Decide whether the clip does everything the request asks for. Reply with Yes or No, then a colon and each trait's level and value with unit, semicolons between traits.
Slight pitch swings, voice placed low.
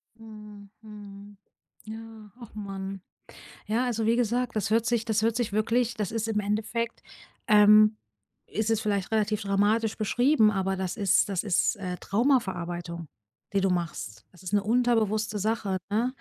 No: narrow, 2.2 semitones; high, 215 Hz